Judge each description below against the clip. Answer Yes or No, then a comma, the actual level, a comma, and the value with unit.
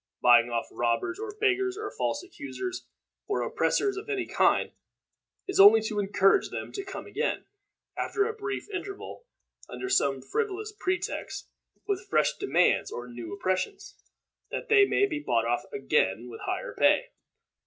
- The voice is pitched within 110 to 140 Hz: No, very high, 370 Hz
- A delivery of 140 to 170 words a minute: Yes, average, 155 wpm